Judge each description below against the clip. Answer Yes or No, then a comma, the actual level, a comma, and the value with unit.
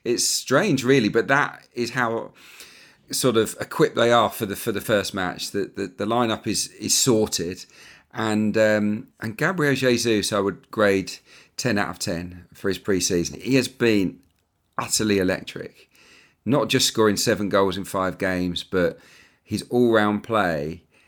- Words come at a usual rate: Yes, average, 170 wpm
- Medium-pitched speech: No, low, 105 Hz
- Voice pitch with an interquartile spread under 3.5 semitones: No, average, 4.2 semitones